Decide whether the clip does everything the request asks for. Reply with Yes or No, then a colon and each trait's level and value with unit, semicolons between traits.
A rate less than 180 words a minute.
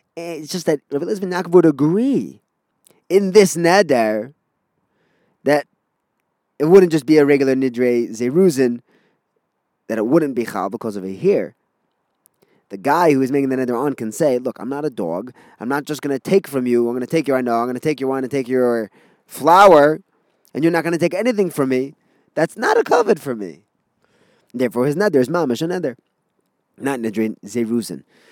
No: average, 185 wpm